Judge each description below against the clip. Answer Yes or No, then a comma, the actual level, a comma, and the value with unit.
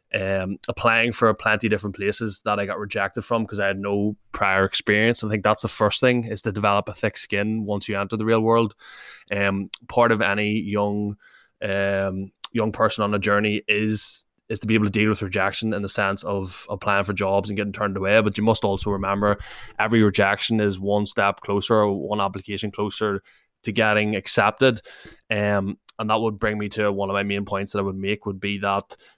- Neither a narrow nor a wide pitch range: No, narrow, 1.5 semitones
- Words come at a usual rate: No, fast, 215 wpm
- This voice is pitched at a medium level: No, low, 105 Hz